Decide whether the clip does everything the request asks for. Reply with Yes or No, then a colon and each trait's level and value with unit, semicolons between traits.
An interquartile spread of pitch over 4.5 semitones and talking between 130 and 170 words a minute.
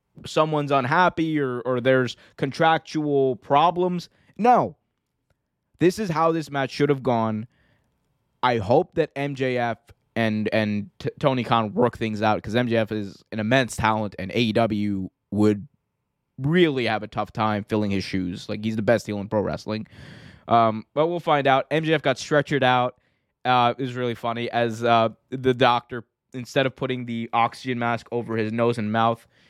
No: average, 4.2 semitones; average, 165 wpm